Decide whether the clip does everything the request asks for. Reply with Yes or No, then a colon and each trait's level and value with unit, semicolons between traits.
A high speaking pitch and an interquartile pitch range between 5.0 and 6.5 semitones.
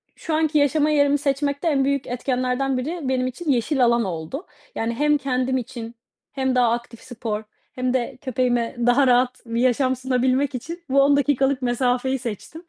No: very high, 260 Hz; narrow, 2.4 semitones